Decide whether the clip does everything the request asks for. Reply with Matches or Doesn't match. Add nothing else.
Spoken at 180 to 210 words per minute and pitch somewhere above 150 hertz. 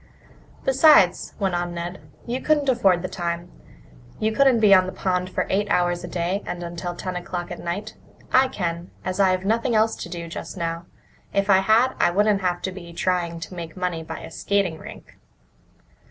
Matches